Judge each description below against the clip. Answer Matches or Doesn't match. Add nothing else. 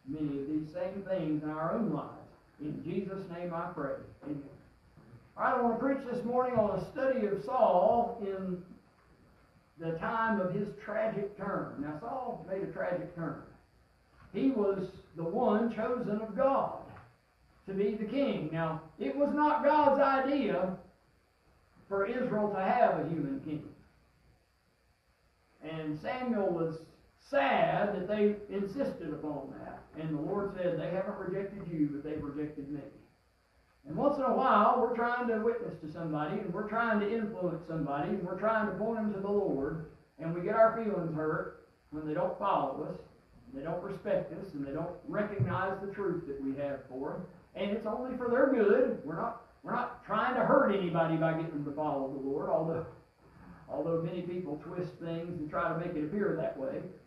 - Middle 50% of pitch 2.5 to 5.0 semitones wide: Doesn't match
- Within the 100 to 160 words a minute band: Doesn't match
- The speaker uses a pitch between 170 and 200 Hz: Matches